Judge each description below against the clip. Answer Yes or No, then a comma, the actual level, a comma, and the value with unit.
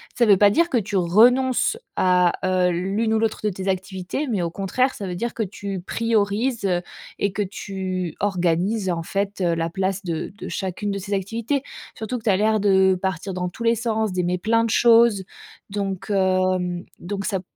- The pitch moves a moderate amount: Yes, average, 3.1 semitones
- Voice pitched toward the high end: Yes, high, 195 Hz